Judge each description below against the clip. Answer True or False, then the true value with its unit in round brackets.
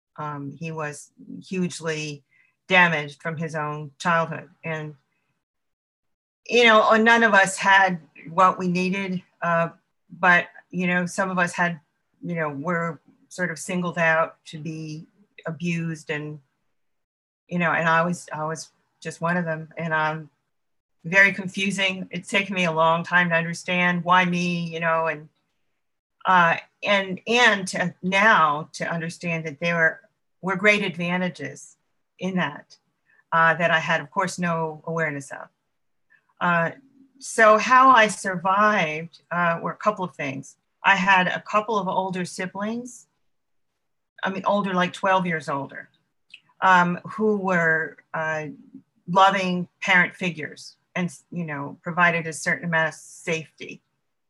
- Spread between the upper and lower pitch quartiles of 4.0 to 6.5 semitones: False (2.9 semitones)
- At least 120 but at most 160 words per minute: True (145 wpm)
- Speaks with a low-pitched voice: False (175 Hz)